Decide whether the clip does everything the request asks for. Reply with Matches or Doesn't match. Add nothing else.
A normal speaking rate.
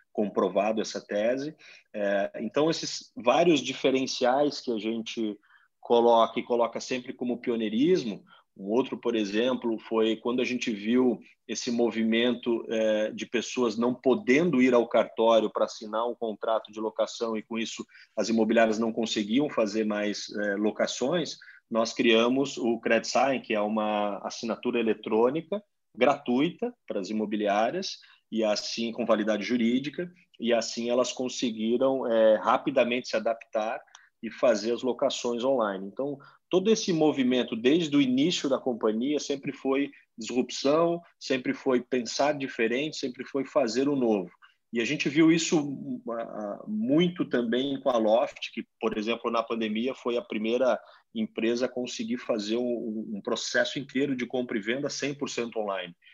Matches